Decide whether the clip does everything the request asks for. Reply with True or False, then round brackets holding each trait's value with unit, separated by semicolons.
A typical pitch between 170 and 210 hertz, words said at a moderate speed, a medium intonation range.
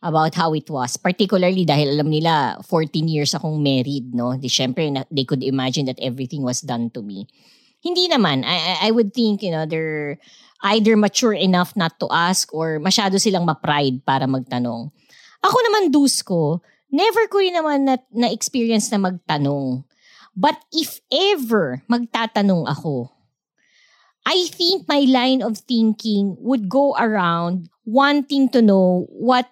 False (185 Hz; 150 wpm; 8.5 semitones)